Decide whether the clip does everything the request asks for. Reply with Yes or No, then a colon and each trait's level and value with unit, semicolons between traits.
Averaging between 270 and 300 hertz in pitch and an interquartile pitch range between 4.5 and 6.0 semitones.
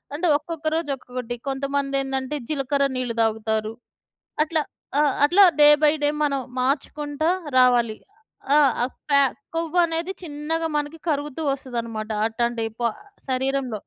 No: very high, 275 Hz; average, 3.3 semitones